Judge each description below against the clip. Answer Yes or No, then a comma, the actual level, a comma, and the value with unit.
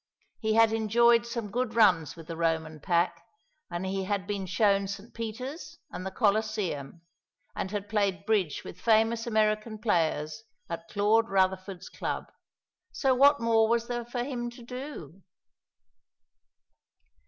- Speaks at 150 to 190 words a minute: No, average, 140 wpm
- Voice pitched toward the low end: No, high, 215 Hz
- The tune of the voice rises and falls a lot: No, average, 3.7 semitones